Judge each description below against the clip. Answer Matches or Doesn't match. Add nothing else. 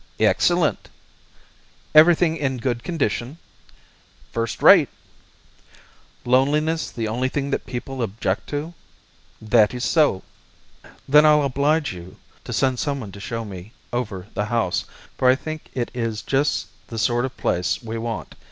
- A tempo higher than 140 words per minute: Doesn't match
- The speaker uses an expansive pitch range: Doesn't match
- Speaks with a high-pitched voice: Doesn't match